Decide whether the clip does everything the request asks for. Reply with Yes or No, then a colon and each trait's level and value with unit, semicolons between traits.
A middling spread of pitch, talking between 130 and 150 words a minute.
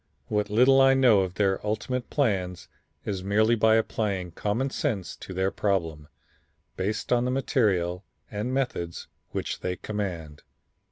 Yes: average, 4.5 semitones; average, 145 wpm